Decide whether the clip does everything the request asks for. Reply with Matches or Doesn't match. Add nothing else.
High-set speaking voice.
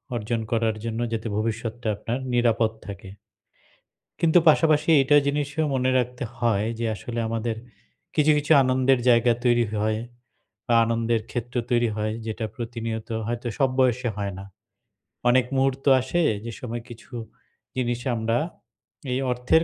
Doesn't match